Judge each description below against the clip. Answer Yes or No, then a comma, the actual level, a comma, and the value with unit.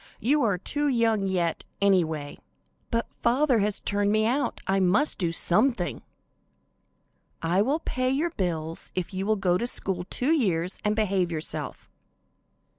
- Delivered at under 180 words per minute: Yes, average, 150 wpm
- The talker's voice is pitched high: Yes, high, 200 Hz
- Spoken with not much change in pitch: No, average, 5.1 semitones